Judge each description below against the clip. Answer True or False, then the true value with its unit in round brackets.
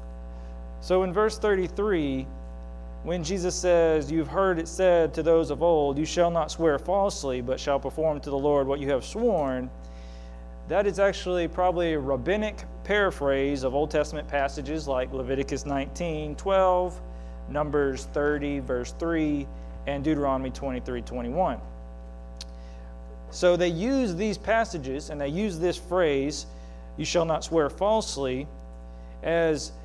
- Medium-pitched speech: True (145 Hz)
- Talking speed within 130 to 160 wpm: True (140 wpm)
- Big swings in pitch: True (5.9 semitones)